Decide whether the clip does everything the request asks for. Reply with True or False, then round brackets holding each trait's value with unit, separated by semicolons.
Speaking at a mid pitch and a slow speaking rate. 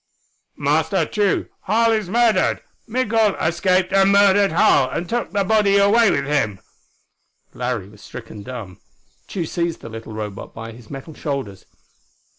False (170 Hz; 145 wpm)